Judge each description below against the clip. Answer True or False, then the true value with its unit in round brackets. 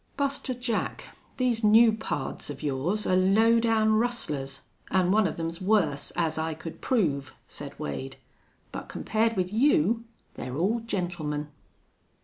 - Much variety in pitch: True (6.7 semitones)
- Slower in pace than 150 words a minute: True (140 wpm)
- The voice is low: False (190 Hz)